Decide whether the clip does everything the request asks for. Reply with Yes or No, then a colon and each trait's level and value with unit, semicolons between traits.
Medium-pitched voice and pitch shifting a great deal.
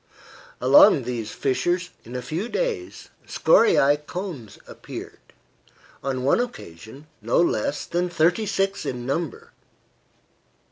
Yes: medium, 155 Hz; wide, 7.4 semitones